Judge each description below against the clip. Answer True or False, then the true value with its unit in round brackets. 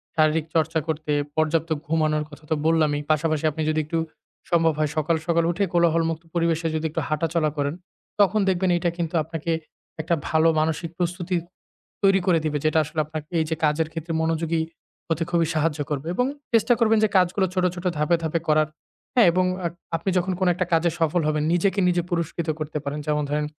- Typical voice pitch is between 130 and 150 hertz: False (165 Hz)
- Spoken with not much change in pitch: True (1.9 semitones)